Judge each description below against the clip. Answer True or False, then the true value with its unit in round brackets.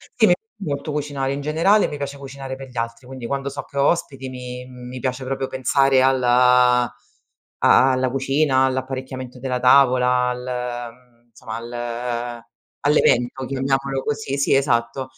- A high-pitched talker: False (130 Hz)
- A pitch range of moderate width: False (1.8 semitones)